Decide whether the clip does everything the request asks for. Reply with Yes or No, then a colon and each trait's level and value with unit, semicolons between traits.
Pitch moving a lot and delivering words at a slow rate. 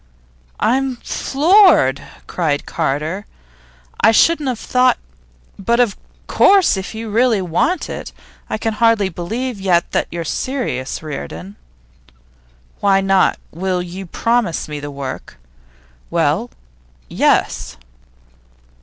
Yes: wide, 6.7 semitones; slow, 110 wpm